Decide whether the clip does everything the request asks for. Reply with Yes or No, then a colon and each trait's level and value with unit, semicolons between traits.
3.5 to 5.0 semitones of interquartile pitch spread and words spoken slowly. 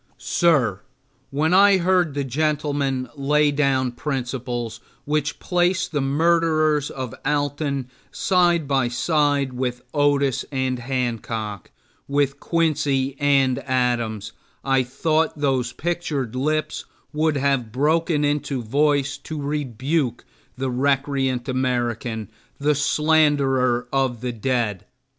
No: average, 3.0 semitones; slow, 110 wpm